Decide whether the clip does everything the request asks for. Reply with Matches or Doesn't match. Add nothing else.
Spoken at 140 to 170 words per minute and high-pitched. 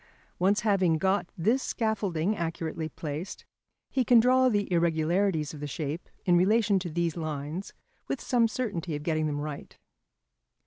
Doesn't match